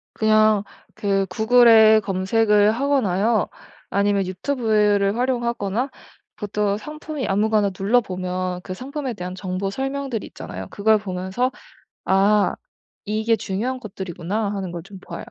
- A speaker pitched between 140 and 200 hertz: No, high, 210 Hz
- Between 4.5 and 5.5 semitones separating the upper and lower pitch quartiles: No, average, 3.3 semitones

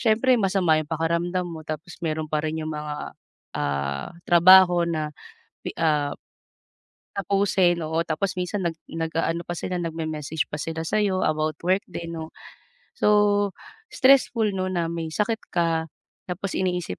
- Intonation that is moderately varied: Yes, average, 3.0 semitones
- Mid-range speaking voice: Yes, medium, 170 Hz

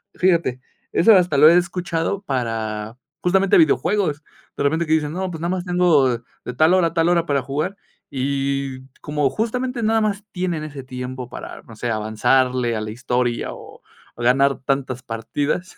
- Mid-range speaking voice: Yes, medium, 145 Hz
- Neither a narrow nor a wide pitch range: No, wide, 5.8 semitones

